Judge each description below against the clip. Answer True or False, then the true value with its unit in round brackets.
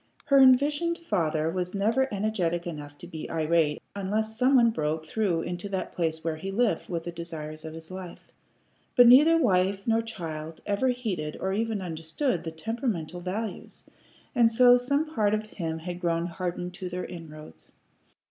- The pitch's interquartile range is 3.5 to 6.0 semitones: True (5.6 semitones)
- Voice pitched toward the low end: False (185 Hz)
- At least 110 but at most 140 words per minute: False (170 wpm)